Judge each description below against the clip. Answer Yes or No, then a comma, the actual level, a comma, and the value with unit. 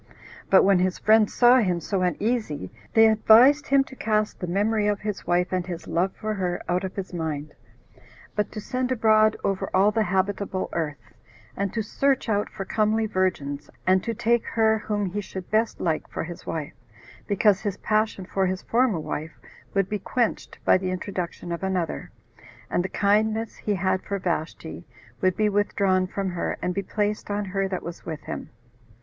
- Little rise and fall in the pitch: No, average, 3.0 semitones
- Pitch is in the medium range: No, high, 195 Hz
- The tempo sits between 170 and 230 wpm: Yes, average, 190 wpm